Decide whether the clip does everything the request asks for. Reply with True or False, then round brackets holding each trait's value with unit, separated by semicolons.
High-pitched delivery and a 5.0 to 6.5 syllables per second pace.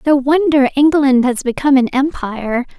True (270 Hz; 5.2 syllables/s)